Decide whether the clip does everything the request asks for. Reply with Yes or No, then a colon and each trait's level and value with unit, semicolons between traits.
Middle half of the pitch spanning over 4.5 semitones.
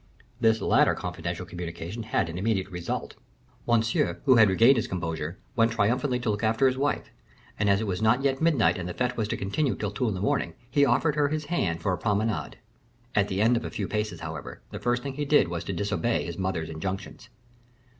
Yes: average, 5.1 semitones